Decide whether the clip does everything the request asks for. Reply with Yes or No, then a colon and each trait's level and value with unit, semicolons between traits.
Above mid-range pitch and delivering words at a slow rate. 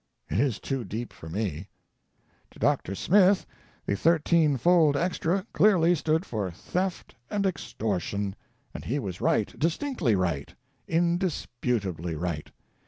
No: low, 135 Hz; slow, 130 wpm